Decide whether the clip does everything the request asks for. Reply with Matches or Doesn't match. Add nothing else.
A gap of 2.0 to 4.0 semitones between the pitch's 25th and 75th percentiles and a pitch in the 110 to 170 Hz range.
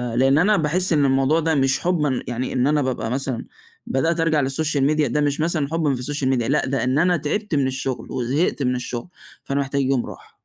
Matches